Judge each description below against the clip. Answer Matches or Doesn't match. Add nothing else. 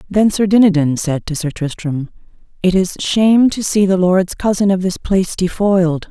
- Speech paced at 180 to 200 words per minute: Matches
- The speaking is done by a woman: Matches